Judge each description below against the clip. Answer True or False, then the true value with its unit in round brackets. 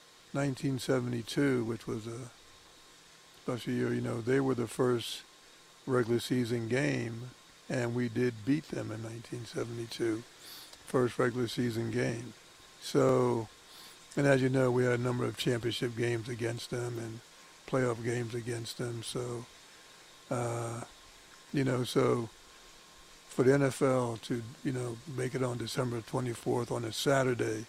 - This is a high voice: False (120 Hz)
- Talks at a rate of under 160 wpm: True (140 wpm)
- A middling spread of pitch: False (1.8 semitones)